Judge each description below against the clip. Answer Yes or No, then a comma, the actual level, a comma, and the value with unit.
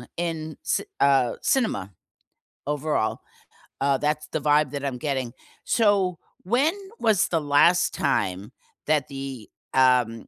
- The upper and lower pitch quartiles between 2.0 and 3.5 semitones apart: No, average, 4.1 semitones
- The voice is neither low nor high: Yes, medium, 145 Hz